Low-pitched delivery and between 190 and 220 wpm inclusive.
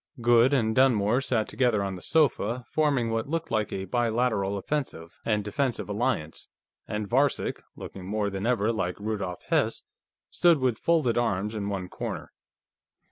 No: low, 110 Hz; average, 155 wpm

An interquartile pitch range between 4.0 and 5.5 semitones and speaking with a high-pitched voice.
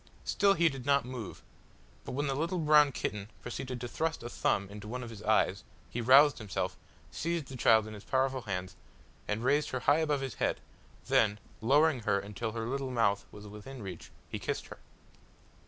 No: average, 4.8 semitones; low, 125 Hz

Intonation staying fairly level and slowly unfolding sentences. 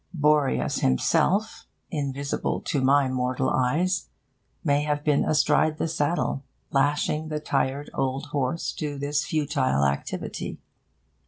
Yes: narrow, 2.1 semitones; slow, 115 wpm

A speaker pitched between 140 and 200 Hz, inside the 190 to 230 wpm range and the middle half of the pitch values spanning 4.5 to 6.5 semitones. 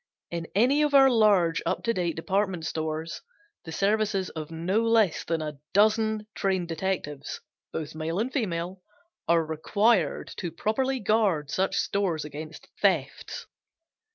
No: medium, 185 Hz; average, 140 wpm; average, 5.0 semitones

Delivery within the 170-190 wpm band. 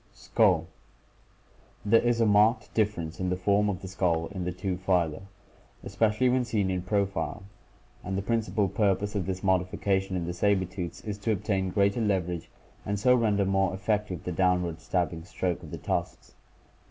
Yes: average, 175 wpm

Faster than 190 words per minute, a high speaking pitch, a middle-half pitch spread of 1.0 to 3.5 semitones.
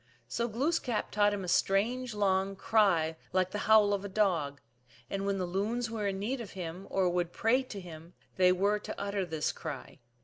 Yes: average, 200 wpm; high, 195 Hz; average, 2.9 semitones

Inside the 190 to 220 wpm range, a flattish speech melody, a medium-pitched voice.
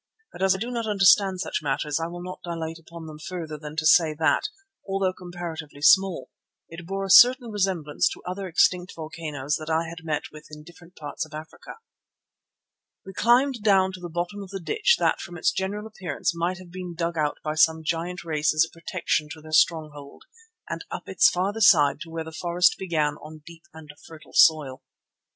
No: average, 200 wpm; average, 3.1 semitones; medium, 170 Hz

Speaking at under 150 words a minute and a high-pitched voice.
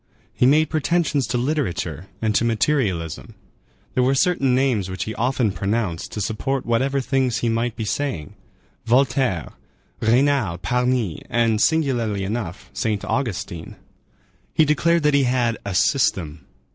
No: slow, 135 wpm; low, 120 Hz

